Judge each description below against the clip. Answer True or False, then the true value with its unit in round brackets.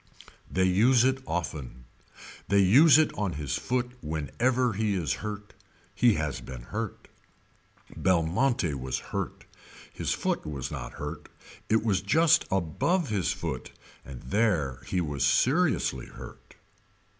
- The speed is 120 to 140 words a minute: True (135 wpm)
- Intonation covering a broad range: True (8.3 semitones)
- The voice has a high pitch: False (95 Hz)